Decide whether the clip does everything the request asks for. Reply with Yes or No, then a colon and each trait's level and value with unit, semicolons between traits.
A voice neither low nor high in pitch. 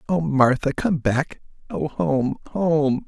Yes: medium, 150 Hz